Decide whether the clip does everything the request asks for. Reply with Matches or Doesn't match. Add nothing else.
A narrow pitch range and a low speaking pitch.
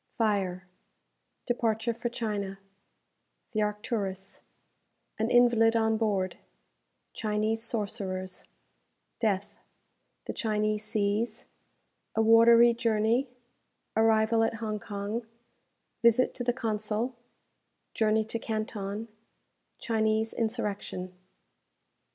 Doesn't match